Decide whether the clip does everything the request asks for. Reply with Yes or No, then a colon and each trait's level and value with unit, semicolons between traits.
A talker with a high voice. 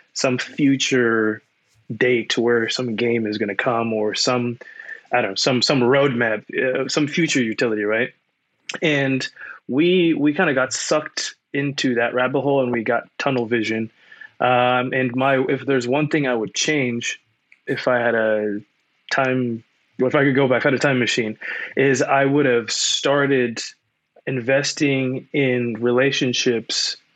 No: low, 130 Hz